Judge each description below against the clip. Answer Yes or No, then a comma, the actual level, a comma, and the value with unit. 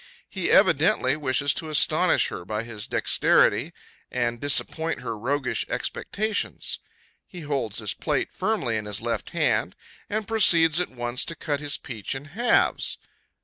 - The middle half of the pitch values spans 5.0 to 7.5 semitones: Yes, wide, 5.5 semitones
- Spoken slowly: No, average, 145 wpm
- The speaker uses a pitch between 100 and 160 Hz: Yes, medium, 140 Hz